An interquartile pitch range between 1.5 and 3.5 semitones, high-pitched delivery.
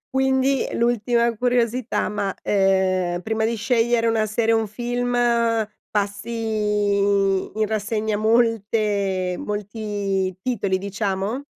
Yes: narrow, 2.6 semitones; high, 215 Hz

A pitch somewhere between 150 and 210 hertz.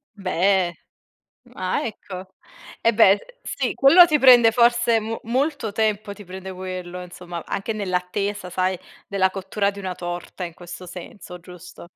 Yes: high, 190 Hz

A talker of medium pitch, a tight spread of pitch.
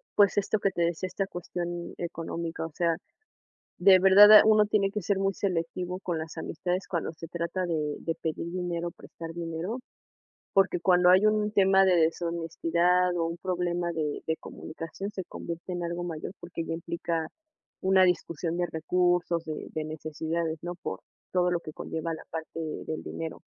Yes: medium, 175 Hz; narrow, 2.0 semitones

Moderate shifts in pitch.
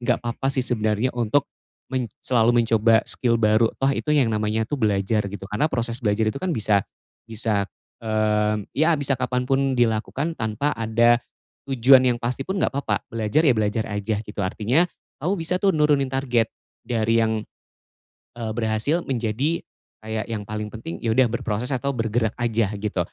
Yes: average, 3.3 semitones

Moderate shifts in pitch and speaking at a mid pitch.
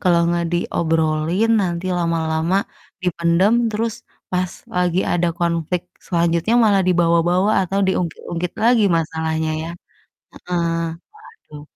No: narrow, 1.7 semitones; medium, 170 Hz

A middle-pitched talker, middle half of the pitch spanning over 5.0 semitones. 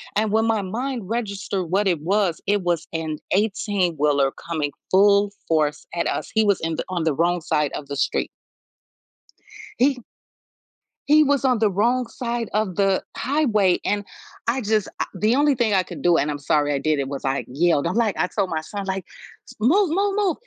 No: high, 200 Hz; wide, 5.6 semitones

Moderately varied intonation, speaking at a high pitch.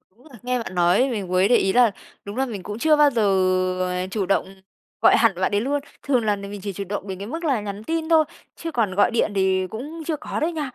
No: wide, 5.8 semitones; high, 220 Hz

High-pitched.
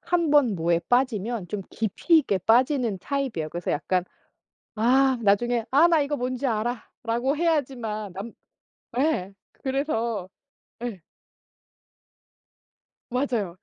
Yes: high, 240 Hz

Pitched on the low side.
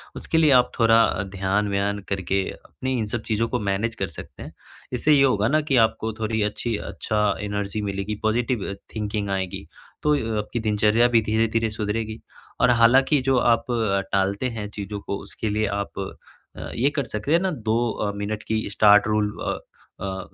Yes: low, 110 Hz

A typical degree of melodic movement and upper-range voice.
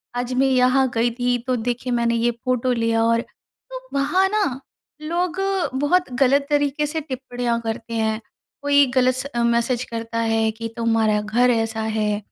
Yes: average, 3.1 semitones; high, 245 Hz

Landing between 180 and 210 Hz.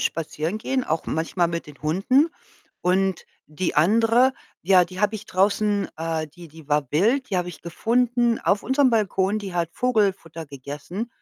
Yes: high, 190 Hz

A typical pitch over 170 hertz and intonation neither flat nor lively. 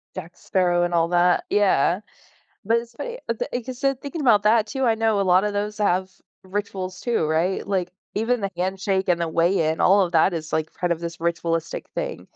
Yes: high, 190 Hz; average, 3.7 semitones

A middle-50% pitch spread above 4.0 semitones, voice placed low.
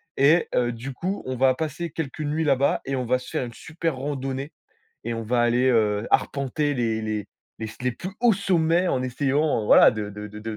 Yes: average, 4.5 semitones; low, 130 Hz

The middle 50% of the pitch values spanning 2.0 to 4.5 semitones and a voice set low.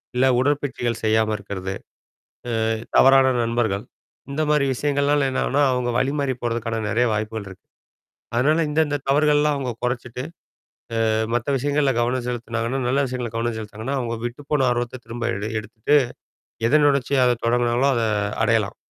Yes: average, 3.2 semitones; low, 120 Hz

